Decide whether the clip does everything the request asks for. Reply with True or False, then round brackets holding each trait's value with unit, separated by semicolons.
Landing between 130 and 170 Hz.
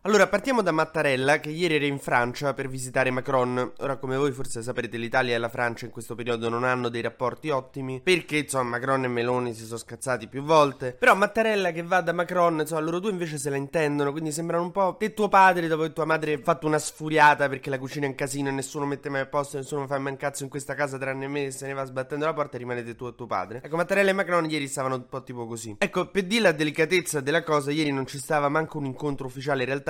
True (140 Hz)